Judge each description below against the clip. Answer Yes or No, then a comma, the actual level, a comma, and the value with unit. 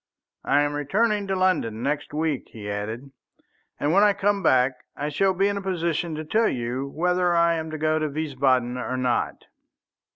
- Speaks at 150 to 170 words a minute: No, average, 190 wpm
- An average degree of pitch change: No, wide, 5.9 semitones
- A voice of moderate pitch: Yes, medium, 155 Hz